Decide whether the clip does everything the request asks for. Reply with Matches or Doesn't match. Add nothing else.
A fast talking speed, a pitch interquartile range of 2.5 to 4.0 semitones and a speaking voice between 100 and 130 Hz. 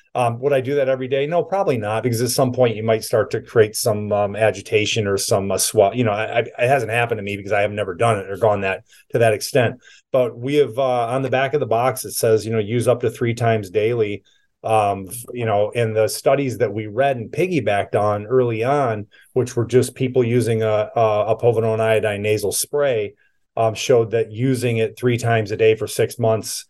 Matches